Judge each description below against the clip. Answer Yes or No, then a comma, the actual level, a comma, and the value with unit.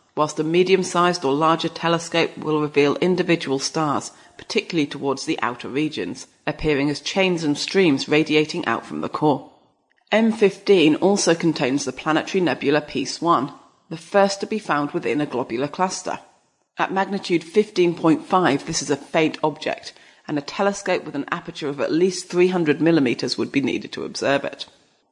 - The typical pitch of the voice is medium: Yes, medium, 165 Hz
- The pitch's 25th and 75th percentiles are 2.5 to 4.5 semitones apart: Yes, average, 3.9 semitones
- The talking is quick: No, average, 165 wpm